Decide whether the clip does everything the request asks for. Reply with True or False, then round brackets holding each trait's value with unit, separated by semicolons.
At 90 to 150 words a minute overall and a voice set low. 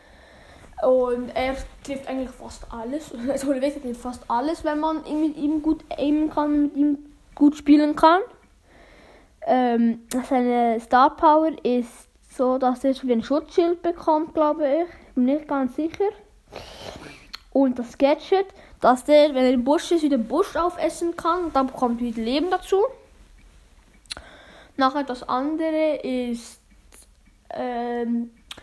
False (140 wpm; 285 Hz)